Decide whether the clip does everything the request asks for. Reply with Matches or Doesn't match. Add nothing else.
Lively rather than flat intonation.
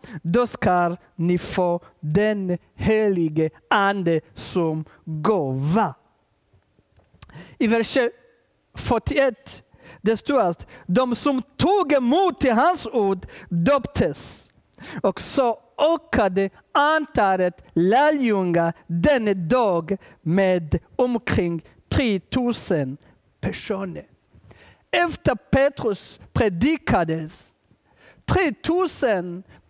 Matches